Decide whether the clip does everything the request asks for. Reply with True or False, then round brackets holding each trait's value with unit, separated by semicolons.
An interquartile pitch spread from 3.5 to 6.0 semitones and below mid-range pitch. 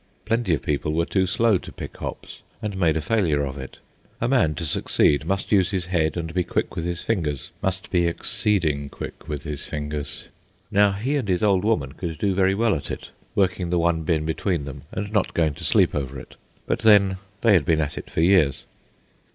True (4.5 semitones; 85 Hz)